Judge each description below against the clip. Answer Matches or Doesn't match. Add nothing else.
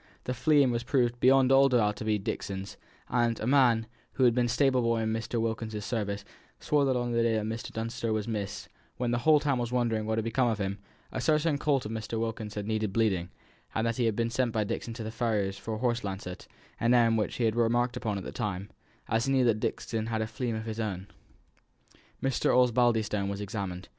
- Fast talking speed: Matches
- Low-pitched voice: Matches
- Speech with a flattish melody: Matches